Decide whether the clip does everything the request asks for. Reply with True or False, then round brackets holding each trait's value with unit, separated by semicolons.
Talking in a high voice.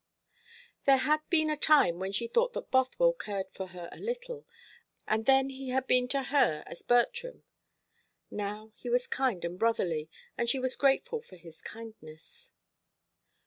True (250 Hz)